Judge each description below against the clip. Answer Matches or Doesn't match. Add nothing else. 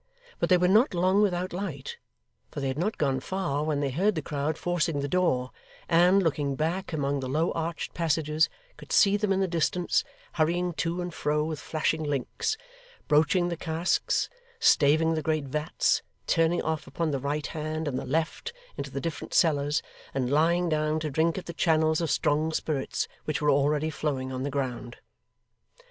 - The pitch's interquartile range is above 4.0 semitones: Doesn't match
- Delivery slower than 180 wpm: Doesn't match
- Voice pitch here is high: Doesn't match